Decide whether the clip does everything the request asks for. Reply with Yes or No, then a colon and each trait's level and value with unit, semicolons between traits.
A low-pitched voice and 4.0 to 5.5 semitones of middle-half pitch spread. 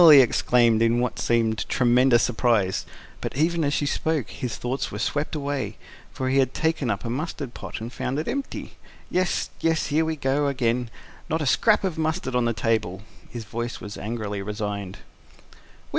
Yes: low, 125 Hz; average, 4.4 semitones